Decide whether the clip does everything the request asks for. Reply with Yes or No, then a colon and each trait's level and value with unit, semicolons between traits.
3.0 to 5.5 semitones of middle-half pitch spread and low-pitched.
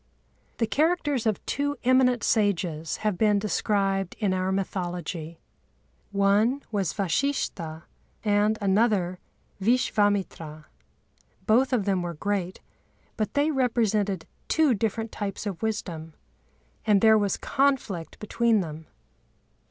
No: average, 3.7 semitones; high, 205 Hz